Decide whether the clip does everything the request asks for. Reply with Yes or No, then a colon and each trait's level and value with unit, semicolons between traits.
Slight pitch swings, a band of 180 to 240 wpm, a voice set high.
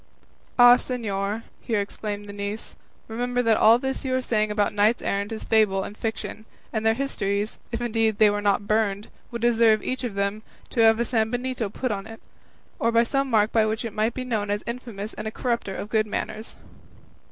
Yes: narrow, 2.3 semitones; average, 200 wpm; high, 220 Hz